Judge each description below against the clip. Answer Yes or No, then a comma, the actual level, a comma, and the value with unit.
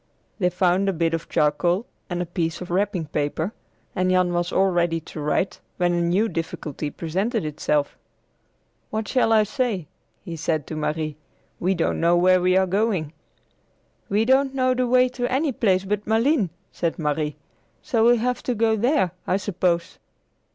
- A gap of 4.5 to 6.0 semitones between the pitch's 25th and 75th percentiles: Yes, average, 5.0 semitones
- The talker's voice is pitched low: No, medium, 185 Hz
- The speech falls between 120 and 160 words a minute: No, average, 175 wpm